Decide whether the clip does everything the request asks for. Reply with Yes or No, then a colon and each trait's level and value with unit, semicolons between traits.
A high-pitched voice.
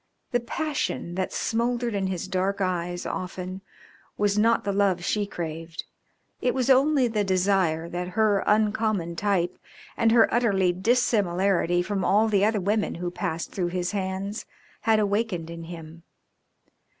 Yes: high, 195 Hz